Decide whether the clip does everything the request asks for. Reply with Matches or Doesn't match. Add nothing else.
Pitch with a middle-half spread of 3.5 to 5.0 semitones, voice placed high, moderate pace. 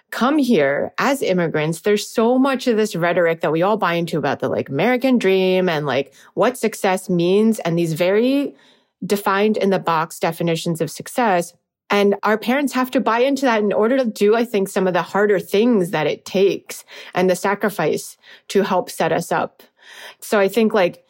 Matches